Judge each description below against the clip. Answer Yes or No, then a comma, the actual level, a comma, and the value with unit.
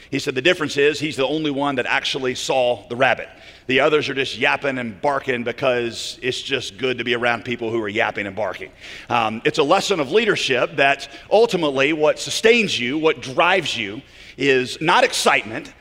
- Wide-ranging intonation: No, average, 3.5 semitones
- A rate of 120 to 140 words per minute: No, average, 195 wpm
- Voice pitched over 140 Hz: No, low, 135 Hz